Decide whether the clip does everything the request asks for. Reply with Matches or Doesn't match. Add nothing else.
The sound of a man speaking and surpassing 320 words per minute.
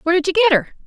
Doesn't match